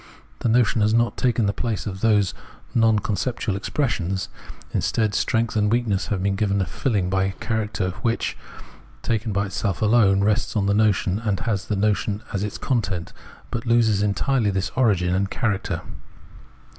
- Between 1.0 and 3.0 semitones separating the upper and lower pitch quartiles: Yes, average, 2.7 semitones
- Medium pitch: No, low, 105 Hz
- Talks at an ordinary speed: Yes, average, 170 wpm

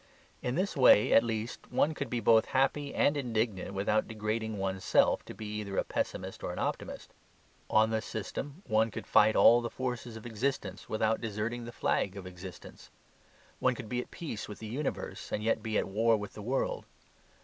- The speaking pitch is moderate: No, low, 110 Hz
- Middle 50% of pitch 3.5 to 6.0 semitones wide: No, narrow, 2.6 semitones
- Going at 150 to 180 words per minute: No, average, 195 wpm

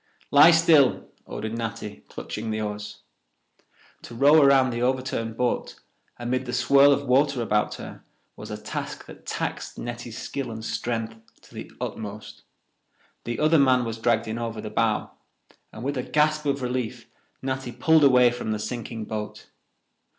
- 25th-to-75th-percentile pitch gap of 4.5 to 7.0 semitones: No, average, 3.5 semitones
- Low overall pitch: Yes, low, 120 Hz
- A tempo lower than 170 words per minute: Yes, average, 160 wpm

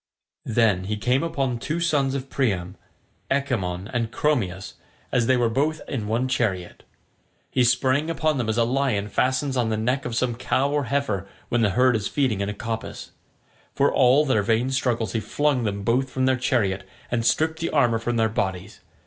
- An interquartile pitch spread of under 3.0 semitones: No, average, 3.7 semitones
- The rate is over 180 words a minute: Yes, average, 190 wpm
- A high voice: No, low, 120 Hz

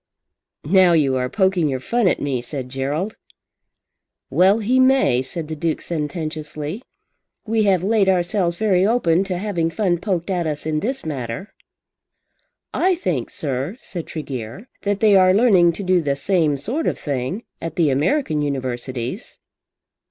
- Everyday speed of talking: Yes, average, 155 wpm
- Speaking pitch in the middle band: Yes, medium, 170 Hz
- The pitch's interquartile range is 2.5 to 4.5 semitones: No, wide, 5.6 semitones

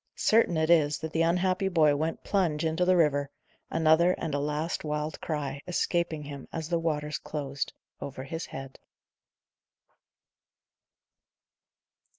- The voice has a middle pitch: Yes, medium, 160 Hz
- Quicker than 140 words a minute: No, slow, 135 wpm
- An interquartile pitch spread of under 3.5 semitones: Yes, narrow, 2.4 semitones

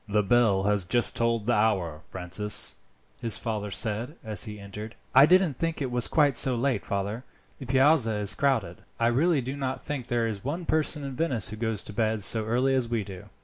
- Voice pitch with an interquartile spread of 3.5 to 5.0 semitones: Yes, average, 4.2 semitones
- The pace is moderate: No, fast, 210 wpm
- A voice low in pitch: Yes, low, 115 Hz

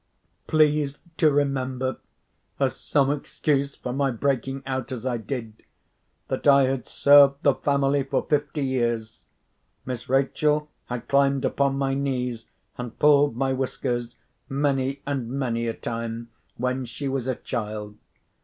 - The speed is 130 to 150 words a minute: Yes, average, 140 wpm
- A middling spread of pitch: No, narrow, 2.3 semitones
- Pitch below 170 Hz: Yes, low, 135 Hz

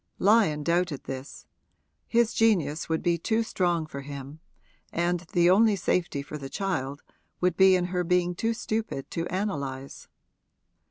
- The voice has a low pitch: No, medium, 175 Hz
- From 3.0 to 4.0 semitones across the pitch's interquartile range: No, average, 4.7 semitones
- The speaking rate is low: No, average, 150 wpm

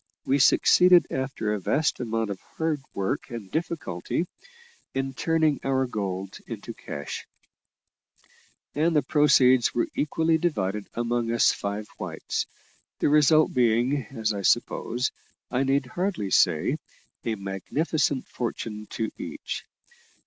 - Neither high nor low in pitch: No, low, 125 Hz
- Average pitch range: No, wide, 5.8 semitones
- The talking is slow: Yes, slow, 125 wpm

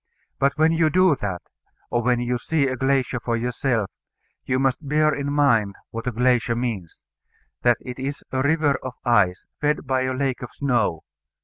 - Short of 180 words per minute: No, average, 185 wpm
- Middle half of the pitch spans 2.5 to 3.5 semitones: Yes, average, 3.0 semitones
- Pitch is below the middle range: Yes, low, 130 Hz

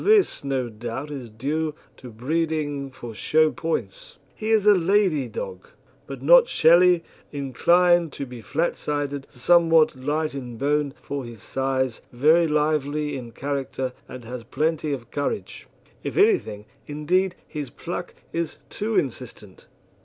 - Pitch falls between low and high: Yes, medium, 145 Hz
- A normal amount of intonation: Yes, average, 4.2 semitones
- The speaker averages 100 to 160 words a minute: Yes, average, 140 wpm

